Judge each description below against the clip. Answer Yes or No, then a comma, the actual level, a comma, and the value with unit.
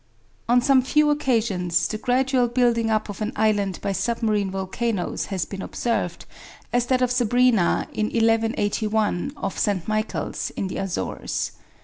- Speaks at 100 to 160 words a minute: Yes, average, 145 wpm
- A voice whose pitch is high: Yes, high, 225 Hz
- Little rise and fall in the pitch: No, average, 3.3 semitones